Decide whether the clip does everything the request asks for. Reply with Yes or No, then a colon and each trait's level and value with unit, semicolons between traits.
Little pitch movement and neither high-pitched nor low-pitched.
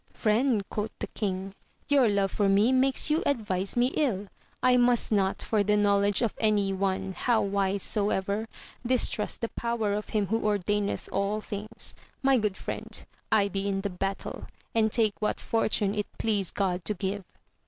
No: narrow, 2.3 semitones; high, 210 Hz